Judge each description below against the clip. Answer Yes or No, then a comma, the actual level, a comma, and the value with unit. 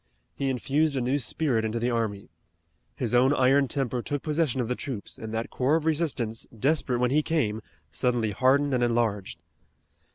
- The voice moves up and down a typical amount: Yes, average, 3.8 semitones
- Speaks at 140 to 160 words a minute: No, average, 175 wpm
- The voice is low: Yes, low, 125 Hz